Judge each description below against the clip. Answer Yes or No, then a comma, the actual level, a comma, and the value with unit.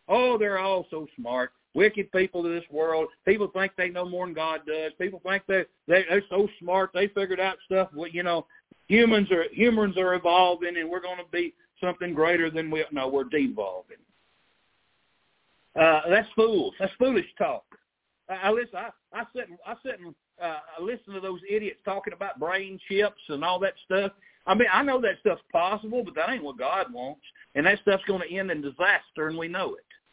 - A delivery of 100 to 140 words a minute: No, fast, 205 wpm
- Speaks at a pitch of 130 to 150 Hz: No, high, 190 Hz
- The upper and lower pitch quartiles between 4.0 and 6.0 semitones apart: No, average, 3.1 semitones